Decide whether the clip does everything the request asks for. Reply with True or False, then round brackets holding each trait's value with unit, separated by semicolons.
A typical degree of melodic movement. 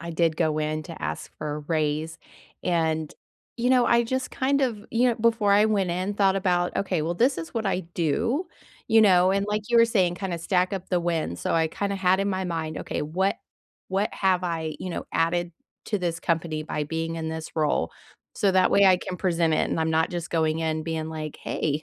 True (3.6 semitones)